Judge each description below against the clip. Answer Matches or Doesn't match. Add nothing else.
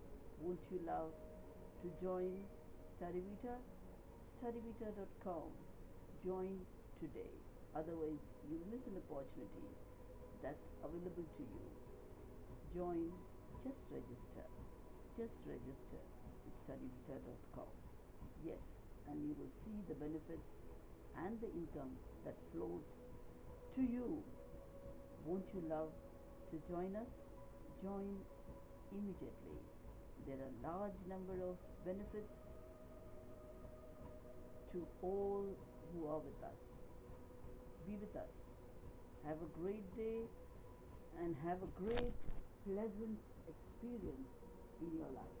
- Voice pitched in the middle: Matches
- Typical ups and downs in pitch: Matches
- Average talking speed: Doesn't match